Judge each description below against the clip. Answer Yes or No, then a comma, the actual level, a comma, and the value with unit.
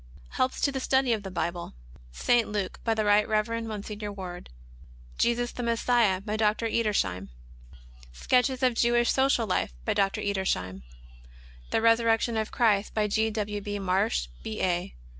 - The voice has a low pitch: No, high, 215 Hz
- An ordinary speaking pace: Yes, average, 160 wpm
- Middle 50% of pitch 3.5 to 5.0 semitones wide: No, average, 3.1 semitones